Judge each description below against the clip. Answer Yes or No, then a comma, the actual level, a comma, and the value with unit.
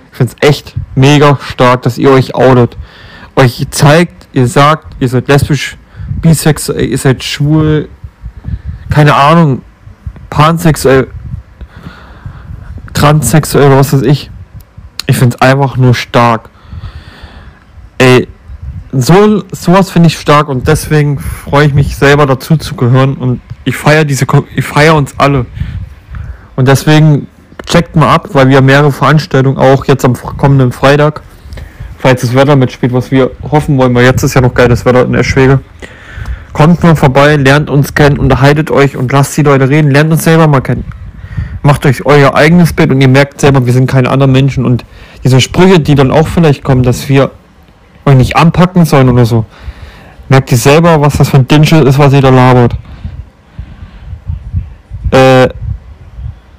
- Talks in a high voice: No, low, 135 Hz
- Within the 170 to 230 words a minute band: No, average, 160 wpm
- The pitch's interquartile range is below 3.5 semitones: No, average, 4.7 semitones